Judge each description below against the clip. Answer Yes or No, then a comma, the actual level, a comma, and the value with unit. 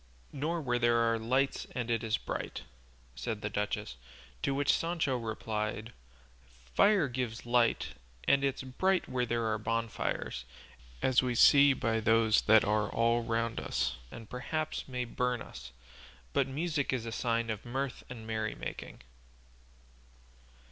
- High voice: No, low, 120 Hz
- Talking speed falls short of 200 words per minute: Yes, average, 145 wpm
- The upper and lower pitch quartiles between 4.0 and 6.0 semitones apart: No, average, 2.8 semitones